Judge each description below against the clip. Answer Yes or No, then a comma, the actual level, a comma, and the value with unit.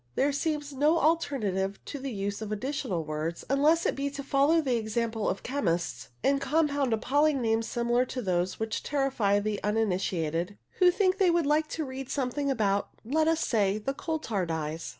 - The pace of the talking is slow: No, average, 185 wpm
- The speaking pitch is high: Yes, very high, 250 Hz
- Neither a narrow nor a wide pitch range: No, wide, 6.1 semitones